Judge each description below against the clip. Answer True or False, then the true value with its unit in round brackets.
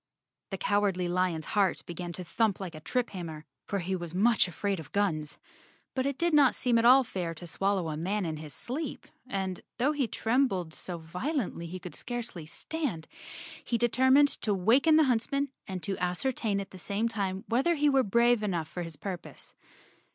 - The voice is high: True (200 Hz)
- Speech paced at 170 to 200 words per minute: True (190 wpm)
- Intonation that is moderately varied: False (5.8 semitones)